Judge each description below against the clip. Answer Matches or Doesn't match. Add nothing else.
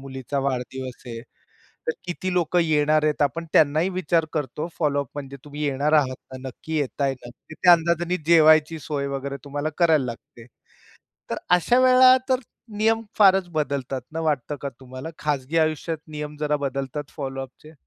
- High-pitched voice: Doesn't match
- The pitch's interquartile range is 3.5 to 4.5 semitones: Doesn't match